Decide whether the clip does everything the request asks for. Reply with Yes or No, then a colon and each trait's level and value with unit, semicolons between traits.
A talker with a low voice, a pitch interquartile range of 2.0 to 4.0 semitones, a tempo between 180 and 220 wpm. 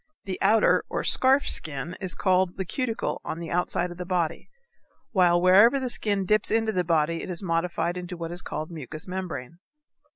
No: medium, 180 Hz; average, 2.8 semitones; average, 190 wpm